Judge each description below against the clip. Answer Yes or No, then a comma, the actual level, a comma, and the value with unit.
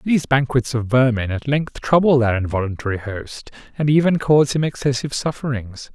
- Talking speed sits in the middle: Yes, average, 160 wpm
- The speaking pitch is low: Yes, low, 130 Hz